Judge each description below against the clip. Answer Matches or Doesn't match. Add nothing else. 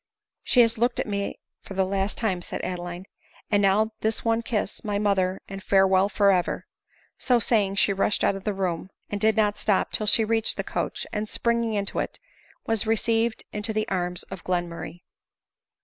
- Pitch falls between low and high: Doesn't match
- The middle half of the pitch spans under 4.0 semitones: Matches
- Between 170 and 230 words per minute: Matches